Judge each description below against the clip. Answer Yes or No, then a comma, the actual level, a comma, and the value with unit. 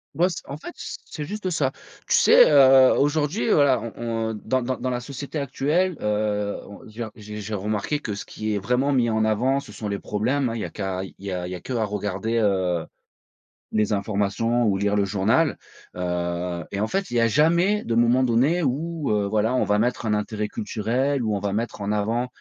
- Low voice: Yes, low, 115 Hz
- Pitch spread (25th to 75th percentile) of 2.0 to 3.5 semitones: No, average, 4.6 semitones